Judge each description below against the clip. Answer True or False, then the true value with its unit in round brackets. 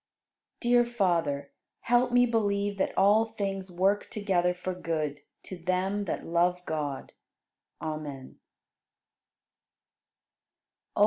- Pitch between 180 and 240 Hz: True (185 Hz)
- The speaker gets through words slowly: True (105 wpm)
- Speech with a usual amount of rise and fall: True (3.6 semitones)